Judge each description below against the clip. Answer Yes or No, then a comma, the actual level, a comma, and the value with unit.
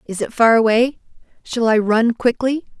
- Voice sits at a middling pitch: No, high, 230 Hz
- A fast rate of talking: No, average, 170 wpm